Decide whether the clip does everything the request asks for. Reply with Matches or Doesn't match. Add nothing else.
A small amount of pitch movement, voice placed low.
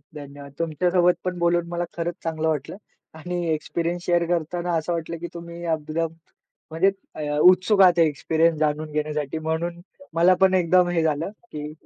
Doesn't match